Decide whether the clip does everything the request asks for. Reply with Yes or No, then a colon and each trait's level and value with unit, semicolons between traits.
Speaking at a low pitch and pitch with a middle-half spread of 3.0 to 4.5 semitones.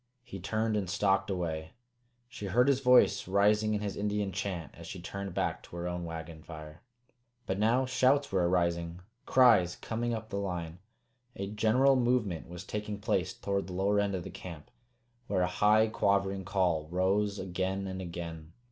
Yes: very low, 95 Hz; average, 3.3 semitones